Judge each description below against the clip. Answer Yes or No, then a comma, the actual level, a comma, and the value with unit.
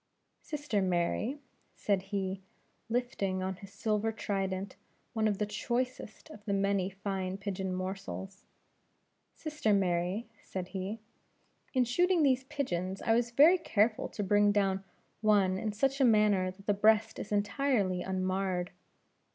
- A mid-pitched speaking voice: No, high, 205 Hz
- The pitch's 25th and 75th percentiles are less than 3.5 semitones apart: Yes, average, 3.0 semitones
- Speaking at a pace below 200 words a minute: Yes, average, 140 wpm